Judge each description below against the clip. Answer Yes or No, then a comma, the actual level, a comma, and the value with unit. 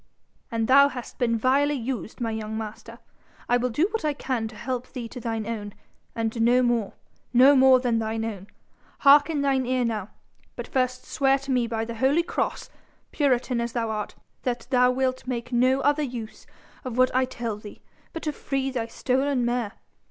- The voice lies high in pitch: Yes, very high, 250 Hz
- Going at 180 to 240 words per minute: Yes, average, 195 wpm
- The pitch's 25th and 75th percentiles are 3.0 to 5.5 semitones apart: No, narrow, 2.6 semitones